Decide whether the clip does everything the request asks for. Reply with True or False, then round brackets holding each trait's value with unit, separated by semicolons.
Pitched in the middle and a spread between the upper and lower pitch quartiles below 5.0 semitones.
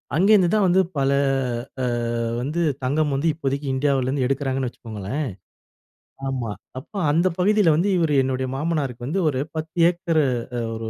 True (145 Hz; 4.3 semitones)